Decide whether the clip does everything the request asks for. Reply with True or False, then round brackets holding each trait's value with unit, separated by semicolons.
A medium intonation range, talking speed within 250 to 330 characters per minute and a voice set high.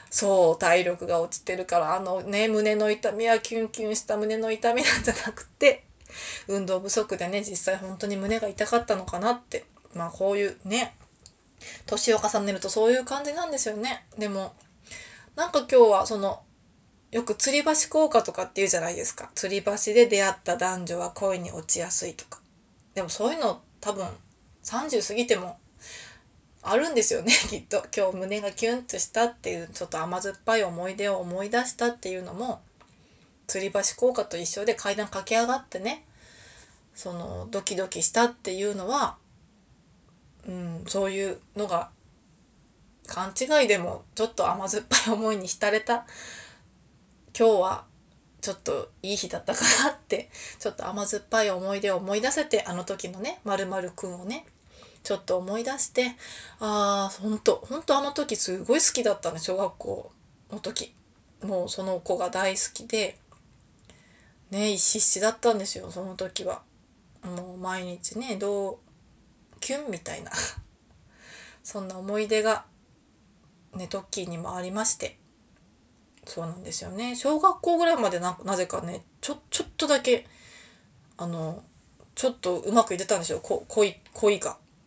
True (3.6 semitones; 315 characters per minute; 205 Hz)